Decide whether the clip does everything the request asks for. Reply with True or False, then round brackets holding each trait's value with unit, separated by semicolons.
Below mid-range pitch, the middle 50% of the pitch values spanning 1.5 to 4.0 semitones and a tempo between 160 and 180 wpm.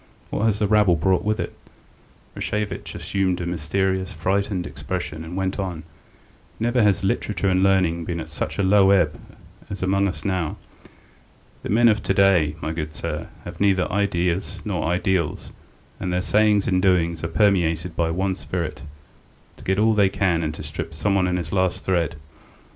True (95 Hz; 2.7 semitones; 175 wpm)